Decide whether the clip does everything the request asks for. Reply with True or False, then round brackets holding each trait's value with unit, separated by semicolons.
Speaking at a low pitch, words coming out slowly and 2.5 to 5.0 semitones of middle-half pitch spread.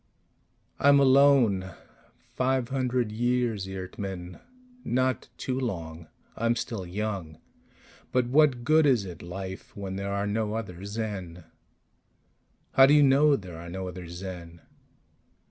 False (105 Hz; 130 wpm; 5.6 semitones)